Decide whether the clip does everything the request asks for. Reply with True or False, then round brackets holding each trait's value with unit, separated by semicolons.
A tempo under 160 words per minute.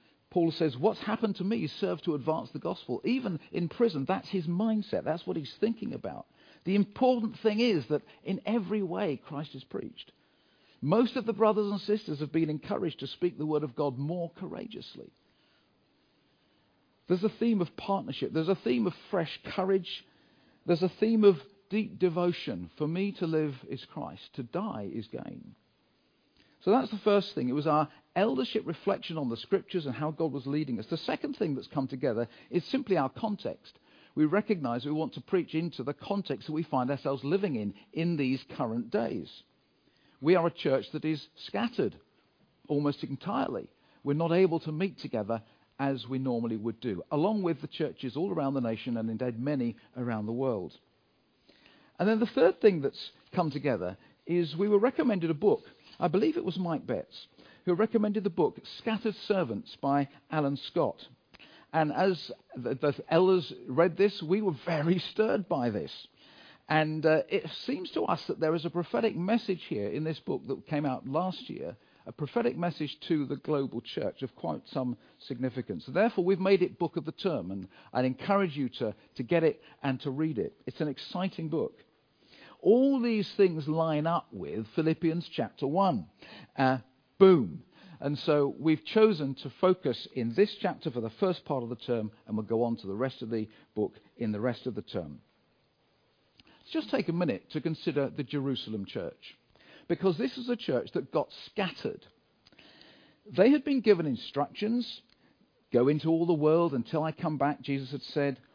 False (185 wpm)